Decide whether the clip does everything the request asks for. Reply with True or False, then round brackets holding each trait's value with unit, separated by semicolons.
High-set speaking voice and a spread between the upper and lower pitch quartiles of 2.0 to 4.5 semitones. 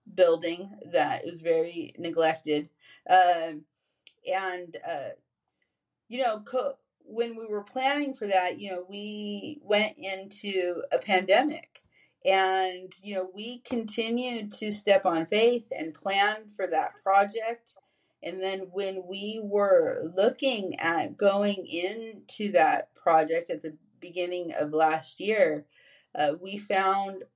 True (200 Hz; 3.9 semitones)